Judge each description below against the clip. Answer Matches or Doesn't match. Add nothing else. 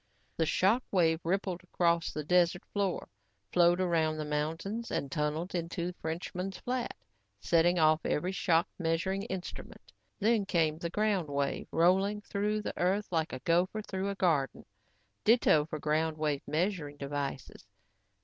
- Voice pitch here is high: Doesn't match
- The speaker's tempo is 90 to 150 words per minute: Matches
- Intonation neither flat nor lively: Matches